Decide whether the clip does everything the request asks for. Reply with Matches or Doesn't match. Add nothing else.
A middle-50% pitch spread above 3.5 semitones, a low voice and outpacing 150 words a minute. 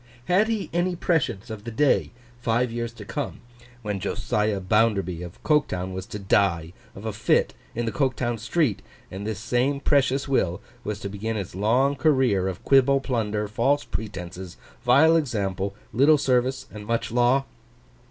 Matches